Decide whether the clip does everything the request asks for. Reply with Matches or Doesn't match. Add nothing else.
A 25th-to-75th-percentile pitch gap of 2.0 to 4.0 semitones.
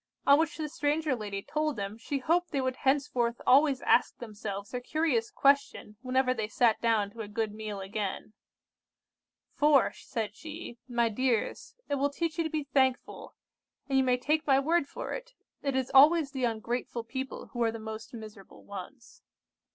Doesn't match